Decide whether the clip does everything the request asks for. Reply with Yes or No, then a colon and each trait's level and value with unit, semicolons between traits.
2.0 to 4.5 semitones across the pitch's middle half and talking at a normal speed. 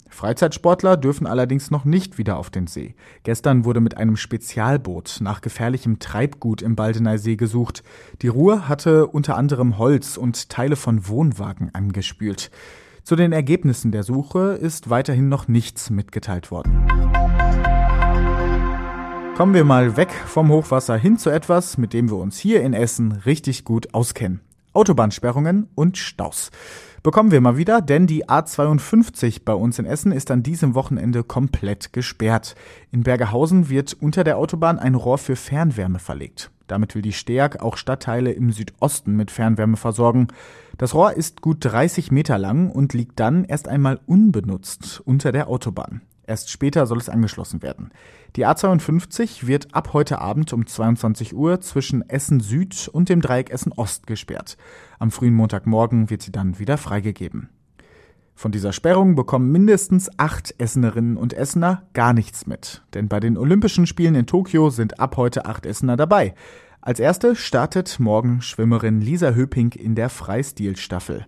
No: wide, 5.6 semitones; average, 155 wpm